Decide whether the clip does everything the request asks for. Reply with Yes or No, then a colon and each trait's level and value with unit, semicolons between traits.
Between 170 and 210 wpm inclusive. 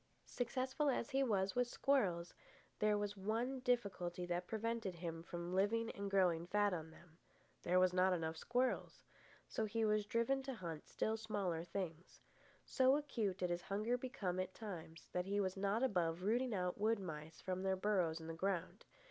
Yes: average, 180 wpm